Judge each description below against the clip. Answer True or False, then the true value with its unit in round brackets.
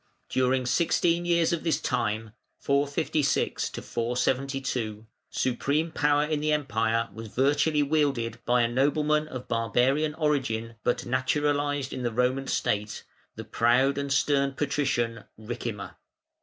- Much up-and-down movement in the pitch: False (3.7 semitones)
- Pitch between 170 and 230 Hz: False (135 Hz)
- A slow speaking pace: True (125 wpm)